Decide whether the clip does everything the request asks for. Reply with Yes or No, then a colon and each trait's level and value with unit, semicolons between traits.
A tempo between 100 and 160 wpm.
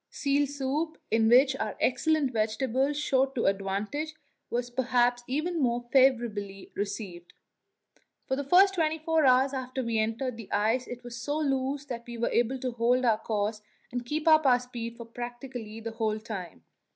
No: average, 175 wpm